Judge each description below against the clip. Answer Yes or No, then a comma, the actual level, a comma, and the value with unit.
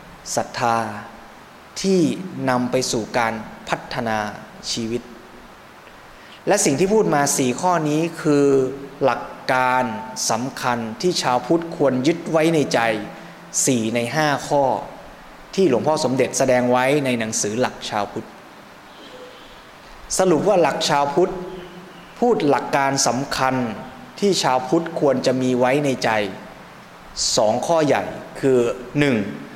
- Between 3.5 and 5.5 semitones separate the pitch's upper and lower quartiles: Yes, average, 4.8 semitones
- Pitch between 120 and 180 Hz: Yes, low, 135 Hz